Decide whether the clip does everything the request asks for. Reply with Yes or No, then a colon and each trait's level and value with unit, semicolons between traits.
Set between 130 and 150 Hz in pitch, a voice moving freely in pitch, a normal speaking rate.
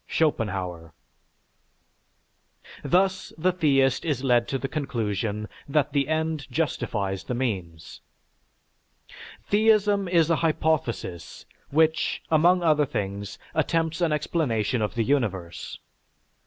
No: medium, 140 Hz; wide, 7.2 semitones; slow, 105 wpm